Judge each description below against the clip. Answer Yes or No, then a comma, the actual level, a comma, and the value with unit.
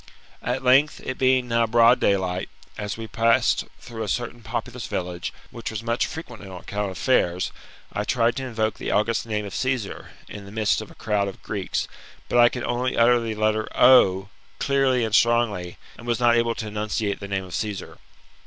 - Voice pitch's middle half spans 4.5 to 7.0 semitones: No, average, 2.8 semitones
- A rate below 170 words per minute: No, average, 200 wpm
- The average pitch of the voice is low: Yes, low, 115 Hz